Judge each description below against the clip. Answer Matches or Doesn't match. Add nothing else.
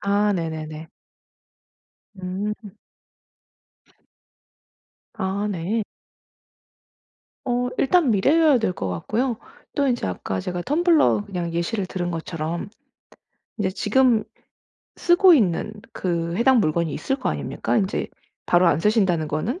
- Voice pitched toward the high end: Matches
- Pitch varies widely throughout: Matches